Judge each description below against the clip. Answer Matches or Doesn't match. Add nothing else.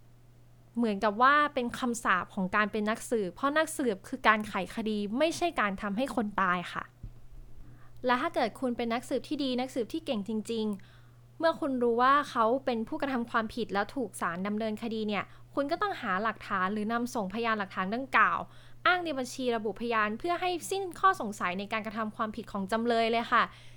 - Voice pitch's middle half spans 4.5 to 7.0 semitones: Doesn't match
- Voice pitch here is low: Doesn't match